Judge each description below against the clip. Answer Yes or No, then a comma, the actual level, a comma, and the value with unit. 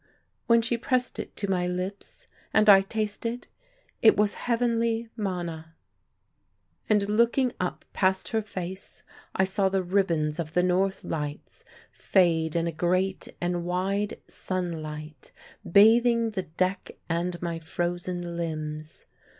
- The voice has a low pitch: No, medium, 185 Hz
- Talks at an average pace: No, slow, 130 wpm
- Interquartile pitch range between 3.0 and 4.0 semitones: Yes, average, 3.7 semitones